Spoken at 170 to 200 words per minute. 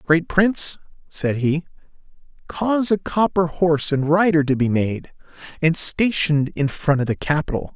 No: average, 155 wpm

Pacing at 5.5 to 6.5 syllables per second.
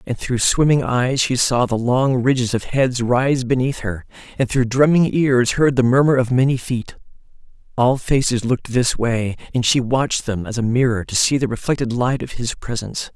No: 5.0 syllables/s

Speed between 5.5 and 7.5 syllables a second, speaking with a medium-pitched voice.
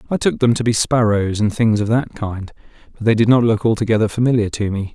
No: 6.0 syllables/s; low, 110 Hz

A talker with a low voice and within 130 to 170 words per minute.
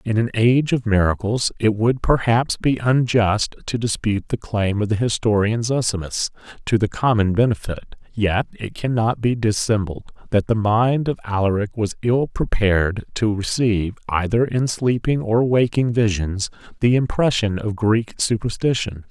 Yes: low, 110 Hz; average, 150 wpm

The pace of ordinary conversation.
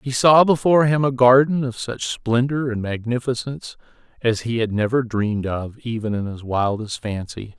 Yes: average, 175 wpm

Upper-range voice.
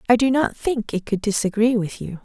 Yes: high, 225 Hz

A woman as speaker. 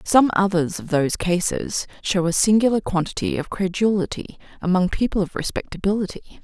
Yes: female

